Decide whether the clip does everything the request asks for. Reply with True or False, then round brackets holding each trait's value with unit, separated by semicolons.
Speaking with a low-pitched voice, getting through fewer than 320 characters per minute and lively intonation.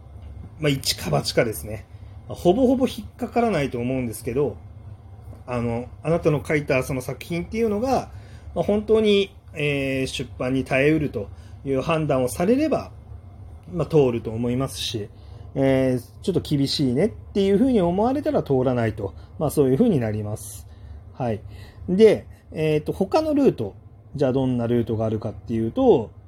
False (125 Hz; 350 characters per minute; 6.9 semitones)